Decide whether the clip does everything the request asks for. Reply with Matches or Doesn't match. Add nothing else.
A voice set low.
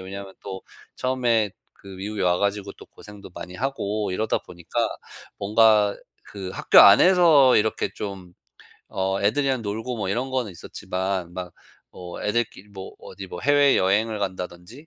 Matches